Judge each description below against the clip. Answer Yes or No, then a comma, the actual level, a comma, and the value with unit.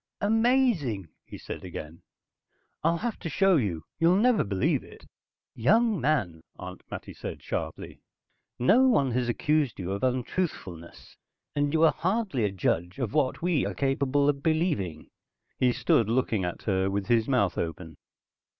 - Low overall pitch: Yes, low, 130 Hz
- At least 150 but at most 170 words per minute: Yes, average, 155 wpm